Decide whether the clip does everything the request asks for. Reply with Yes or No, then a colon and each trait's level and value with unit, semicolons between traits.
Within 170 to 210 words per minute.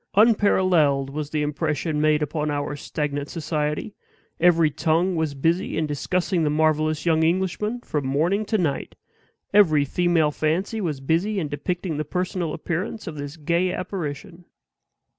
No: average, 145 wpm